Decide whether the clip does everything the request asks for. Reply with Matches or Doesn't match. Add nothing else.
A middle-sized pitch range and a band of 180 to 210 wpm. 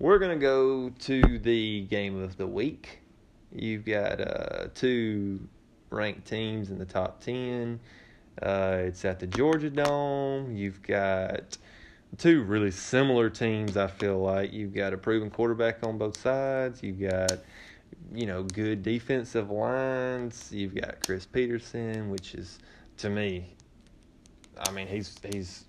Doesn't match